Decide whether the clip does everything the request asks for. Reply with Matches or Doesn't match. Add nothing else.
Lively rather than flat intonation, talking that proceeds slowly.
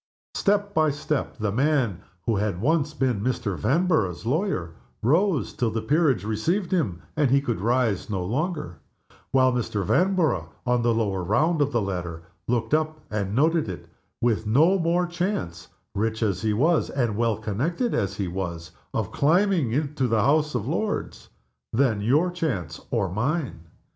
Doesn't match